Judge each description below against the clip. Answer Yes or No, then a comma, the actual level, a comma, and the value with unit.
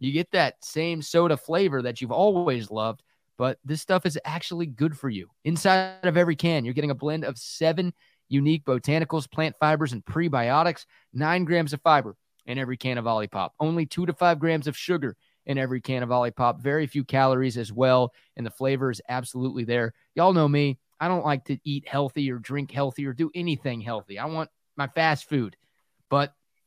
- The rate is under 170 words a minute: No, average, 200 wpm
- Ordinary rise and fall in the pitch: Yes, average, 4.0 semitones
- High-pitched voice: No, medium, 140 Hz